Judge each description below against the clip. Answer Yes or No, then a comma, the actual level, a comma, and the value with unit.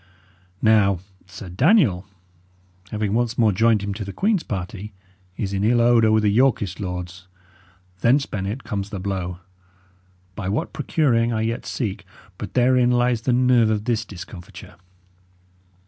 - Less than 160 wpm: Yes, average, 145 wpm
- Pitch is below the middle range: Yes, low, 110 Hz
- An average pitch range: Yes, average, 3.6 semitones